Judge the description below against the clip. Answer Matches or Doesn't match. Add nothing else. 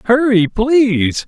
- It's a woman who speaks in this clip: Doesn't match